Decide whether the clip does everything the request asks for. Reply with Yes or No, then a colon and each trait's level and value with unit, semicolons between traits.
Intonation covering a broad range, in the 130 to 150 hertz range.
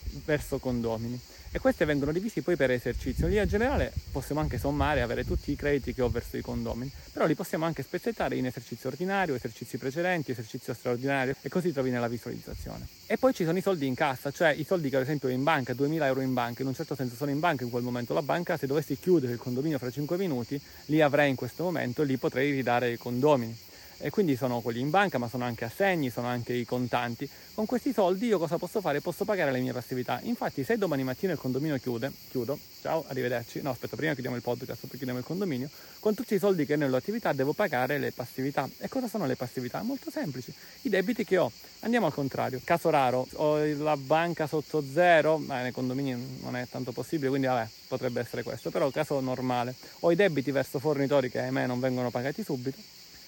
No: average, 4.6 semitones; medium, 140 Hz